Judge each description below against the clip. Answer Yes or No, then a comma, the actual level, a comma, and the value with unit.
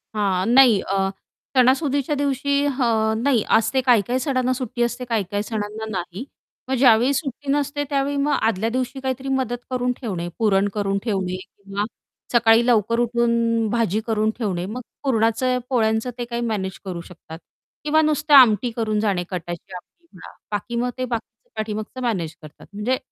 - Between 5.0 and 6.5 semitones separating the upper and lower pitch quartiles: No, average, 3.7 semitones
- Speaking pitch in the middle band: No, high, 230 Hz